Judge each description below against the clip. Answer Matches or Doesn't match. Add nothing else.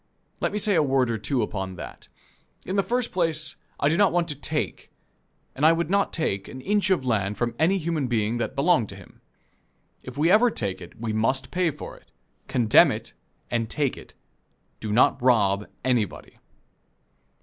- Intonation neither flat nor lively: Doesn't match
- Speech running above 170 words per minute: Matches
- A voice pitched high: Doesn't match